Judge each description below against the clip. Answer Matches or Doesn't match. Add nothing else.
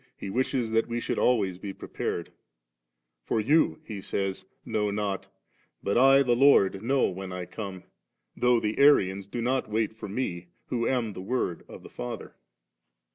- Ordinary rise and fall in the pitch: Matches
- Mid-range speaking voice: Doesn't match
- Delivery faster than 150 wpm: Matches